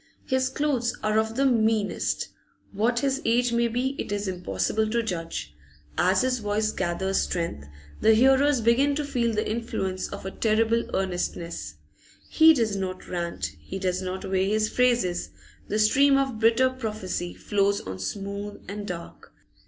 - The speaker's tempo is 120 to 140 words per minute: No, average, 160 wpm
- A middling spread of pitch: Yes, average, 4.3 semitones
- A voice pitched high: Yes, high, 215 Hz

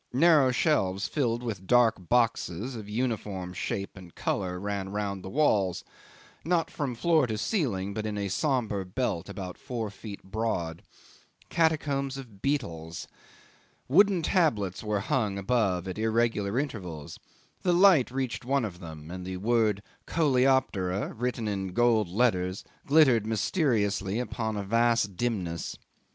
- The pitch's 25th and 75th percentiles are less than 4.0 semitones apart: No, average, 4.9 semitones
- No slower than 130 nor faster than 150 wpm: Yes, average, 140 wpm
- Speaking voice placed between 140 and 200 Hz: No, low, 110 Hz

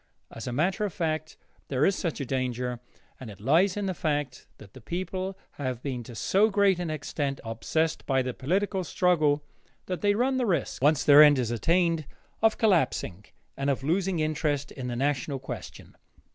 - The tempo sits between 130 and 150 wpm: No, average, 185 wpm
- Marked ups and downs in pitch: Yes, wide, 5.9 semitones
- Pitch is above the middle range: No, medium, 155 Hz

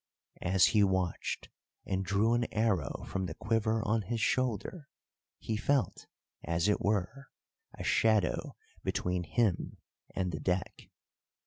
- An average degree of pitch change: Yes, average, 3.6 semitones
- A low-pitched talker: Yes, low, 105 Hz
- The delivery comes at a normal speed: No, slow, 130 wpm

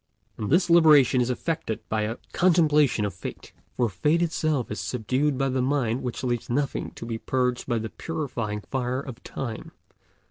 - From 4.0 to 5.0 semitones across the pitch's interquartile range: Yes, average, 4.3 semitones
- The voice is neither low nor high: No, low, 130 Hz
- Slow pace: No, average, 175 wpm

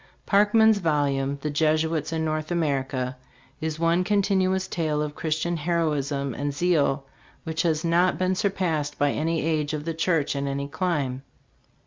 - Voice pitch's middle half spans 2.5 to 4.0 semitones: Yes, average, 3.0 semitones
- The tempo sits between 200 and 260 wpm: No, average, 155 wpm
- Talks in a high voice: No, medium, 155 Hz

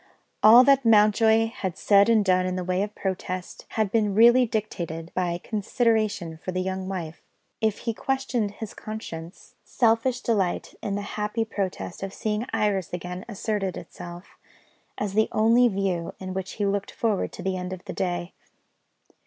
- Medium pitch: No, high, 200 Hz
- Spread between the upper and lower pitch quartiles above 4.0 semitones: No, average, 3.1 semitones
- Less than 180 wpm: Yes, average, 170 wpm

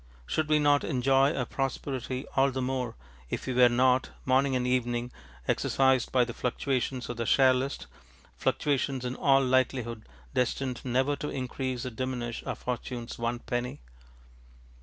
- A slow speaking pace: No, average, 155 wpm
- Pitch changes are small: Yes, narrow, 1.6 semitones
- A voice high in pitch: No, low, 130 Hz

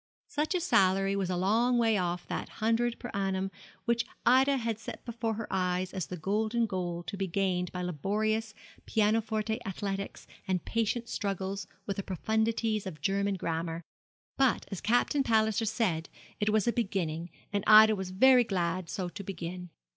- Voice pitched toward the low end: No, high, 200 Hz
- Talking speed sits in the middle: Yes, average, 170 wpm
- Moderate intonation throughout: Yes, average, 3.3 semitones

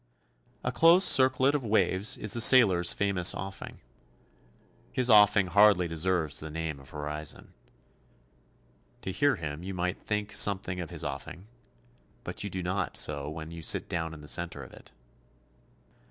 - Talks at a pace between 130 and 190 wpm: Yes, average, 155 wpm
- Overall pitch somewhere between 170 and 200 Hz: No, very low, 90 Hz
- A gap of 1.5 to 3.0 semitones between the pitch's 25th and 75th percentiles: No, average, 4.4 semitones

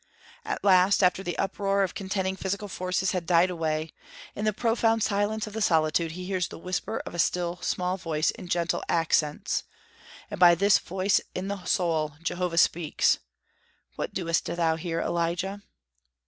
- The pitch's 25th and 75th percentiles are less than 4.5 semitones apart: Yes, average, 2.7 semitones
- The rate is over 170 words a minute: No, average, 165 wpm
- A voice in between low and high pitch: Yes, medium, 180 Hz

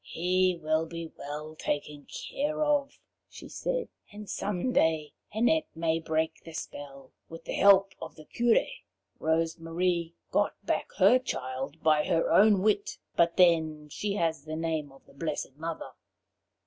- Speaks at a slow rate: No, average, 150 wpm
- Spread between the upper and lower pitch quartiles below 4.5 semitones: Yes, average, 4.0 semitones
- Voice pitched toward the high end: No, medium, 165 Hz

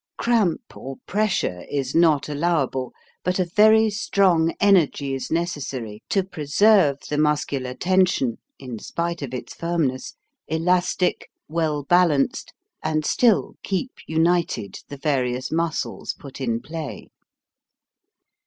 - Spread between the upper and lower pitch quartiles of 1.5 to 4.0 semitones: No, average, 4.8 semitones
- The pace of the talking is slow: Yes, slow, 115 wpm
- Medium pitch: Yes, medium, 160 Hz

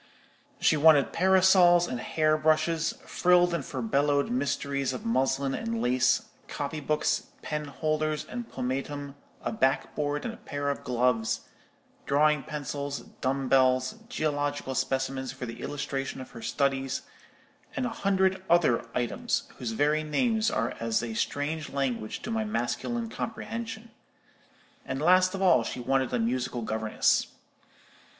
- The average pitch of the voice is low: No, medium, 145 Hz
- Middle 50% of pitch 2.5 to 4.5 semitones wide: No, average, 5.0 semitones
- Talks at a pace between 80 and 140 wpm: Yes, slow, 135 wpm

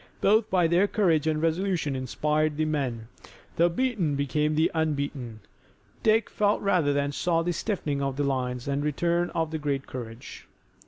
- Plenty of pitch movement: No, average, 3.7 semitones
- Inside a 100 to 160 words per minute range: No, average, 170 wpm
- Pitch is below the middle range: No, medium, 155 Hz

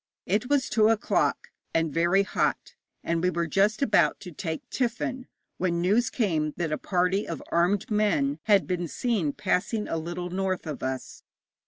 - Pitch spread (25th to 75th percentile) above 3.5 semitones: Yes, average, 4.1 semitones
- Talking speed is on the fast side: No, average, 170 wpm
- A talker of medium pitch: Yes, medium, 180 Hz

